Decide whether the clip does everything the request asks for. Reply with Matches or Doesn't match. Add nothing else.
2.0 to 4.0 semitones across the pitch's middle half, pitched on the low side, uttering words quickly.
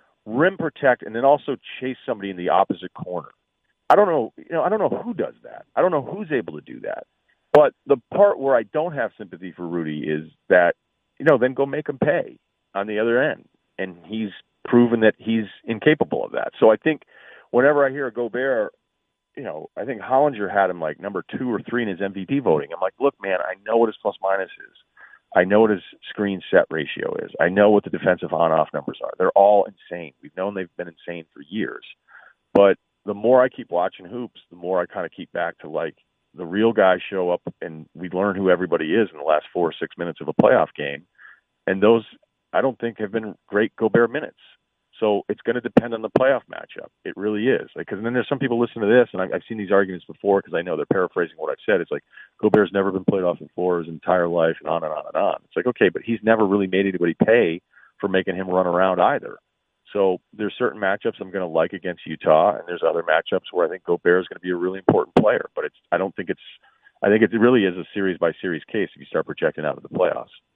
Doesn't match